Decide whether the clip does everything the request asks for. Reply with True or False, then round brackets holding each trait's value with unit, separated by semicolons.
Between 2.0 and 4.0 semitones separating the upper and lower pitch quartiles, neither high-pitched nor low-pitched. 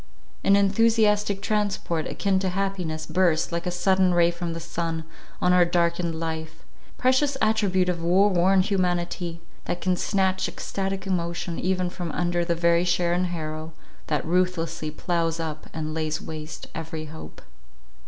True (2.4 semitones; 175 Hz)